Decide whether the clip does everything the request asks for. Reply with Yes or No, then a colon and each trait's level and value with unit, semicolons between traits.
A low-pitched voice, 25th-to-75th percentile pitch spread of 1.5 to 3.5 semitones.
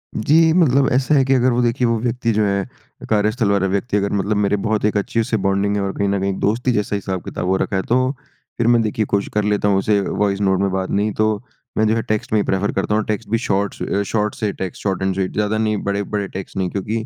Yes: low, 105 Hz; narrow, 2.4 semitones